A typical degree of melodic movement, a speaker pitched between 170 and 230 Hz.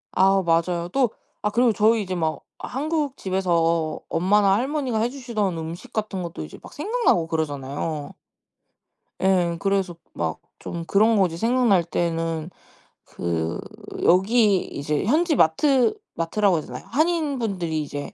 No: wide, 5.9 semitones; high, 190 Hz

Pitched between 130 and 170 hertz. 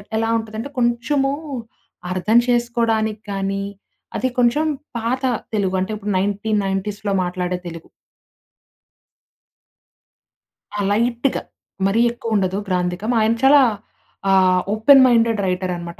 No: high, 215 Hz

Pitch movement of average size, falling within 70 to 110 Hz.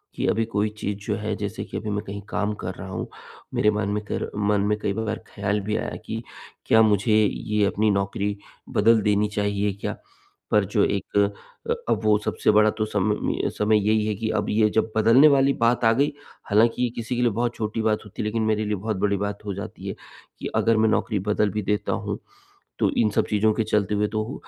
No: narrow, 1.3 semitones; low, 105 Hz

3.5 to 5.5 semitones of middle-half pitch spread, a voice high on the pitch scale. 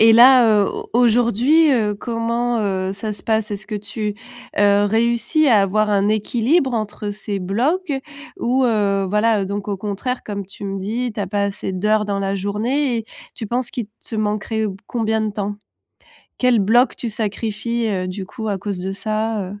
No: average, 2.7 semitones; high, 215 Hz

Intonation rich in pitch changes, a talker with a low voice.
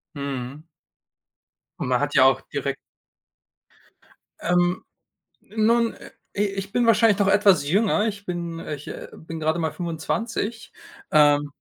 No: wide, 5.8 semitones; medium, 175 Hz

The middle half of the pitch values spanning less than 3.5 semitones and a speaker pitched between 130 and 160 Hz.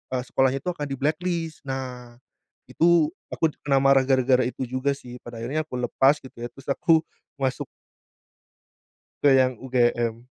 Yes: average, 2.8 semitones; low, 135 Hz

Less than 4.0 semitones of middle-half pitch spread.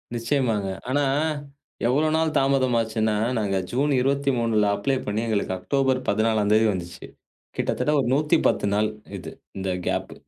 No: average, 4.4 semitones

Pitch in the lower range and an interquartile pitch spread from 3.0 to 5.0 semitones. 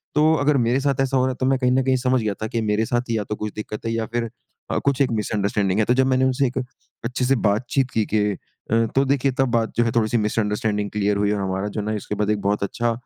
Yes: low, 115 Hz; average, 3.7 semitones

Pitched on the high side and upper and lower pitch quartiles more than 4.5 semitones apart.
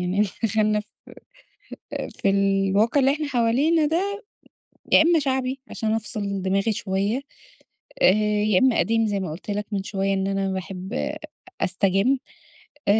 Yes: high, 210 Hz; average, 4.9 semitones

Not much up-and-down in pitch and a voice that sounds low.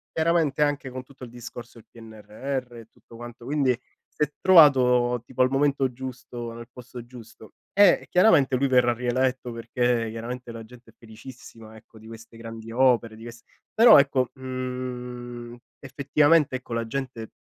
Yes: narrow, 2.2 semitones; low, 125 Hz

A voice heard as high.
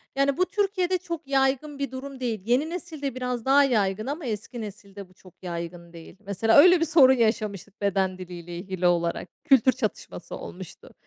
Yes: high, 240 Hz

